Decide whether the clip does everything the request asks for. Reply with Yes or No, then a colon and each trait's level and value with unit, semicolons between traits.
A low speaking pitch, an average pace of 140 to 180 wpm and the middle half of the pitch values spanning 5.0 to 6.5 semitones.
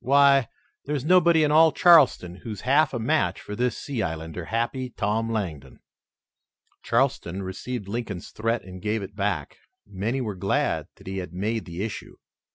Yes: low, 110 Hz; average, 165 wpm; wide, 5.6 semitones